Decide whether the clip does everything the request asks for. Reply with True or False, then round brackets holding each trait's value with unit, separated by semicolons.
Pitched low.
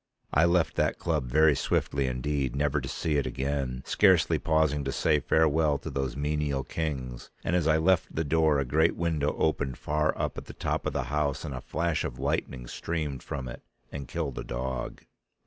True (75 Hz)